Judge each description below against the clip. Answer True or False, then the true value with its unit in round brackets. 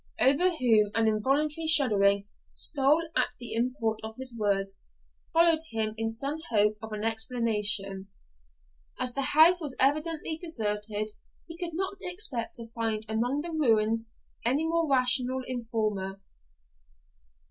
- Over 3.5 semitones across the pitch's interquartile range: True (5.6 semitones)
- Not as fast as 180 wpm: True (135 wpm)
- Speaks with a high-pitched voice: True (235 Hz)